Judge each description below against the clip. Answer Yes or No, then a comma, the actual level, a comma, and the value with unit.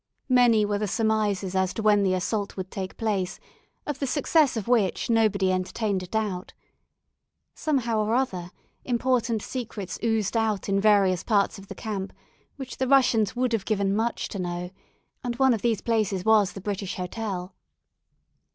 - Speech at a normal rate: Yes, average, 170 wpm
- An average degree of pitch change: Yes, average, 3.3 semitones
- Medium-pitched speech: No, high, 215 Hz